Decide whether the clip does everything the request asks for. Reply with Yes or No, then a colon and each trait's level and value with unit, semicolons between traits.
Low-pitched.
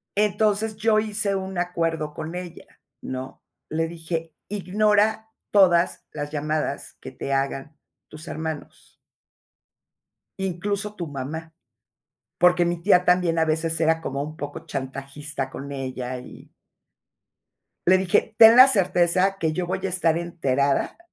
No: medium, 170 Hz